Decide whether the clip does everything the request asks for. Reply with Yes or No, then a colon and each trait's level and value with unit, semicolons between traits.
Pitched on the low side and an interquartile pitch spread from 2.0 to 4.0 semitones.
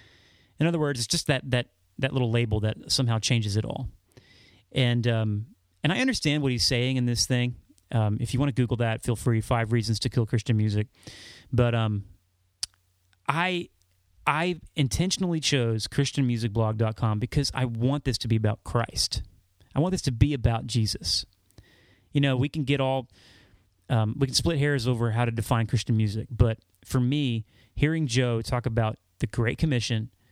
Yes: low, 120 Hz; average, 3.7 semitones